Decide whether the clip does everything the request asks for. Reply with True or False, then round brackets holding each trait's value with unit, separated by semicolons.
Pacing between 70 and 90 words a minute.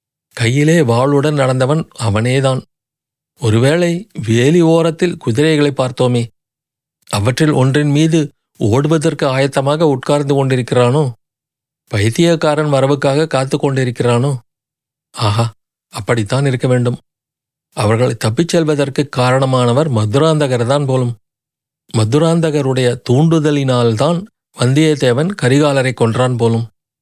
True (80 wpm)